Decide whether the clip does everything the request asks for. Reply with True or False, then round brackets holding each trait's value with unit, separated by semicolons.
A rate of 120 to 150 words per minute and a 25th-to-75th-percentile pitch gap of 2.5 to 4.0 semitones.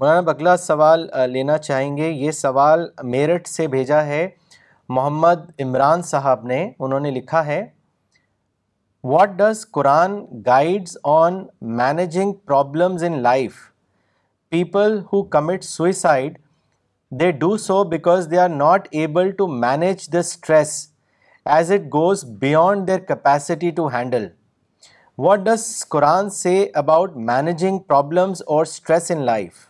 False (130 wpm; 4.4 semitones)